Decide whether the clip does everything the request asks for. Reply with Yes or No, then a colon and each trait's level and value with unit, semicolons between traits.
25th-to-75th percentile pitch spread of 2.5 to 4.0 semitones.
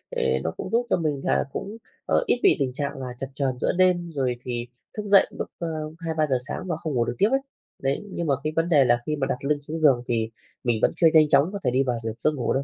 No: average, 4.7 semitones